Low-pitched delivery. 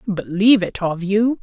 No: high, 200 Hz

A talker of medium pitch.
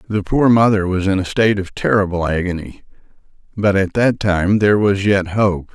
No: low, 100 Hz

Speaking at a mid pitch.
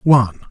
No: low, 125 Hz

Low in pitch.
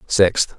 Yes: very low, 95 Hz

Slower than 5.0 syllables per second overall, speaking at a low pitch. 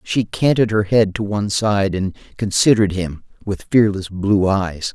Yes: 4.6 syllables/s; low, 100 Hz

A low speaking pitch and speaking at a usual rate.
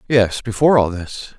Yes: low, 115 Hz; average, 175 wpm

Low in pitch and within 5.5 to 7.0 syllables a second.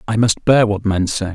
No: low, 105 Hz; 5.0 syllables/s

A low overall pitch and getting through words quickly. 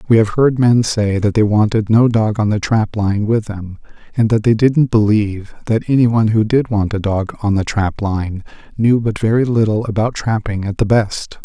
Yes: low, 110 Hz; fast, 220 wpm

